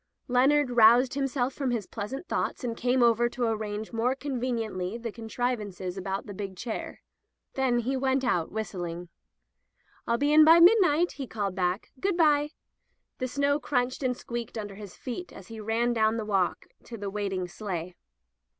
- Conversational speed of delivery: Yes, average, 170 wpm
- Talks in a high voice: Yes, high, 235 Hz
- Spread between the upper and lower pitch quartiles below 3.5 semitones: No, average, 4.2 semitones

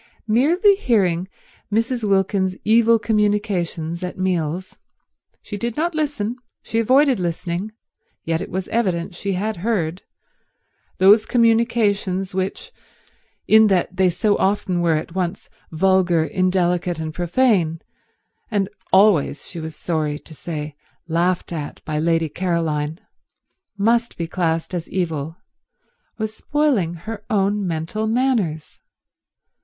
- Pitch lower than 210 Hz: Yes, medium, 185 Hz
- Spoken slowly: Yes, slow, 115 wpm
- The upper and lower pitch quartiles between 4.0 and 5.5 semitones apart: Yes, average, 4.4 semitones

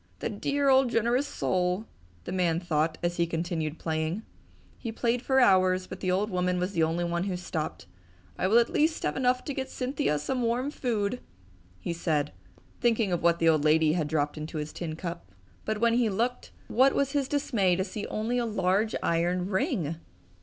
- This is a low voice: No, medium, 185 Hz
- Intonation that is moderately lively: No, wide, 6.1 semitones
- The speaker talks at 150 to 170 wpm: No, average, 200 wpm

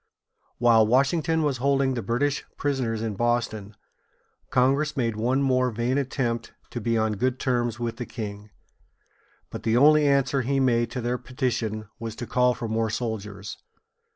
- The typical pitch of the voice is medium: No, low, 120 Hz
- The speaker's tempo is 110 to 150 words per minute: No, average, 160 wpm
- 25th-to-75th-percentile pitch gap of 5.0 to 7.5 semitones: No, average, 2.8 semitones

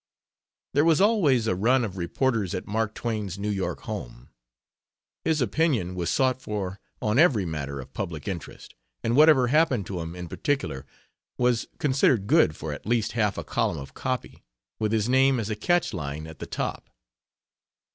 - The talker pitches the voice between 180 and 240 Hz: No, low, 110 Hz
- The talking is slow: No, average, 175 wpm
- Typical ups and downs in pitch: No, wide, 6.6 semitones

